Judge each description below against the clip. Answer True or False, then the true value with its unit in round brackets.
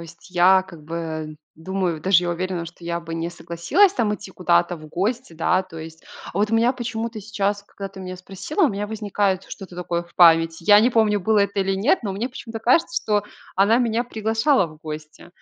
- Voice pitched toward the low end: False (190 Hz)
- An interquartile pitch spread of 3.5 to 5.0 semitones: True (4.3 semitones)